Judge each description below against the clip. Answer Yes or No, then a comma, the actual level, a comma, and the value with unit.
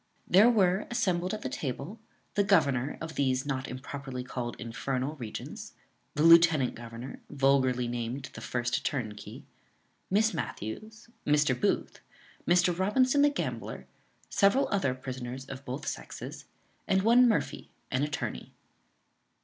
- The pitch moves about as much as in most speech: No, wide, 6.9 semitones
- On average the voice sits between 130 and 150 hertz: Yes, medium, 140 Hz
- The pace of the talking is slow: Yes, slow, 130 wpm